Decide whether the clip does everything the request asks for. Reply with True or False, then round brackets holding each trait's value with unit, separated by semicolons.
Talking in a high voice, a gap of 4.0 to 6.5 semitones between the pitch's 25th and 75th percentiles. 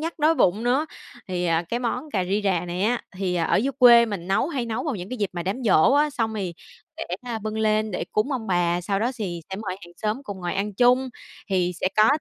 True (215 Hz; 5.0 semitones)